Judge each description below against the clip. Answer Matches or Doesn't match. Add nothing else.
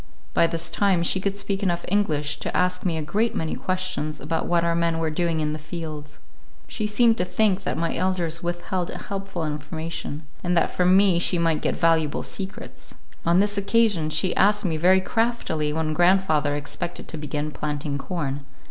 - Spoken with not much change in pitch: Doesn't match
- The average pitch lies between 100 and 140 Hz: Doesn't match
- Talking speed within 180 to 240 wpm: Matches